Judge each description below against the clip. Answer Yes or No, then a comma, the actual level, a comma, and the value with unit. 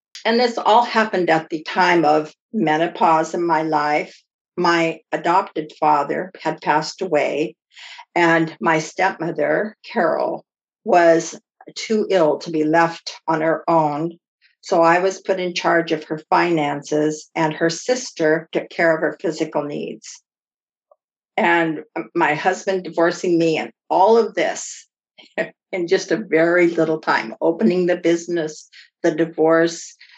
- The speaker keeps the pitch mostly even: Yes, narrow, 2.3 semitones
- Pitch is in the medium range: Yes, medium, 165 Hz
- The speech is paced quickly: No, slow, 135 wpm